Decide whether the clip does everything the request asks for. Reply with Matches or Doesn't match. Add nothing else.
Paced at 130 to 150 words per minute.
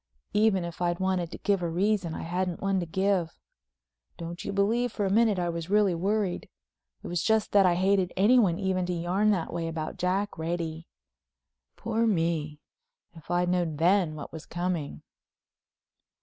Doesn't match